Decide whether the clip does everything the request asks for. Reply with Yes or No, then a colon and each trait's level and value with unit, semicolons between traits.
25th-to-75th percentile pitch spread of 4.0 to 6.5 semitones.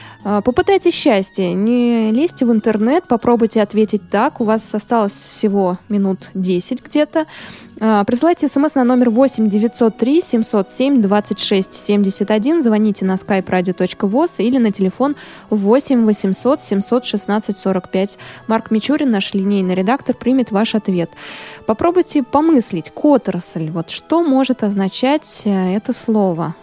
Yes: average, 4.5 semitones